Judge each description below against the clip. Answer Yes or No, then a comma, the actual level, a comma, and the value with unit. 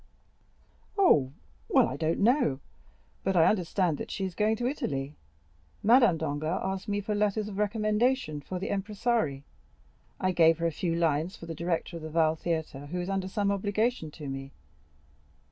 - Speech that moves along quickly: No, average, 175 wpm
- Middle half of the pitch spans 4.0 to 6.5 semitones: Yes, average, 4.8 semitones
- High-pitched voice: No, medium, 180 Hz